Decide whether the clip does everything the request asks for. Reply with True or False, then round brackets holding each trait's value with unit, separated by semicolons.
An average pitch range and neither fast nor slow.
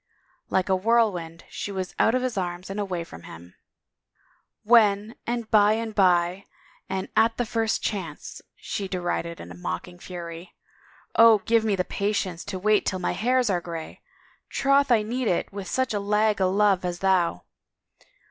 True (3.8 semitones; 175 wpm)